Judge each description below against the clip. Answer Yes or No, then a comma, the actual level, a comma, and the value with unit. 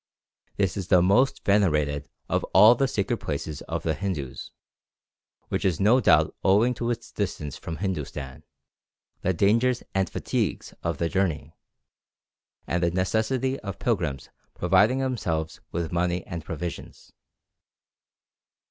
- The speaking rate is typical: No, slow, 130 wpm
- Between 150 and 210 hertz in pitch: No, very low, 95 Hz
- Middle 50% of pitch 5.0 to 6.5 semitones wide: Yes, average, 5.3 semitones